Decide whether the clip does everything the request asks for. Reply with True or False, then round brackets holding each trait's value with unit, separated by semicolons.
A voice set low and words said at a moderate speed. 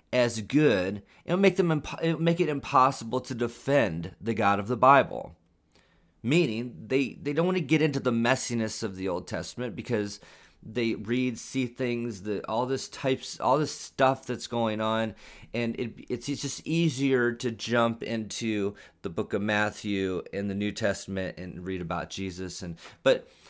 True (120 Hz; 180 wpm)